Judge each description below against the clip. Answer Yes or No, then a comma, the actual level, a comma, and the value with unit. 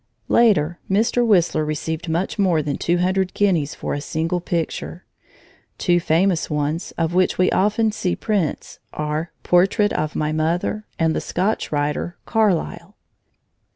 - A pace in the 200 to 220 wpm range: No, average, 145 wpm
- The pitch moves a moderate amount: Yes, average, 3.6 semitones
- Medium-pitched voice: Yes, medium, 175 Hz